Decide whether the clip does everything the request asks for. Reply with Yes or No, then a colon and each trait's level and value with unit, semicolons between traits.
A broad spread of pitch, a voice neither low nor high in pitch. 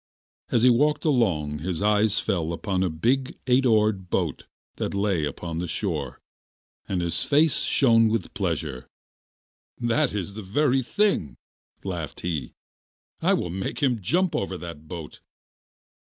No: wide, 6.3 semitones; low, 100 Hz